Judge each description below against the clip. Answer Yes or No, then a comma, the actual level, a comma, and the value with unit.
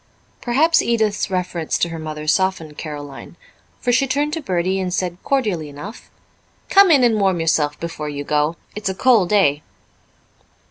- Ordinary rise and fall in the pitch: No, wide, 7.0 semitones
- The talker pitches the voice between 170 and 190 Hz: Yes, medium, 185 Hz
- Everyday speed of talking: Yes, average, 160 wpm